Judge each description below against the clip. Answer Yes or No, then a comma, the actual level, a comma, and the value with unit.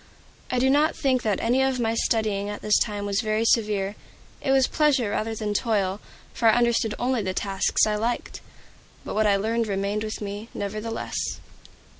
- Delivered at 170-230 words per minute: Yes, average, 185 wpm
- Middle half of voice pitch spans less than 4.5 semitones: Yes, narrow, 2.6 semitones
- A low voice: No, high, 220 Hz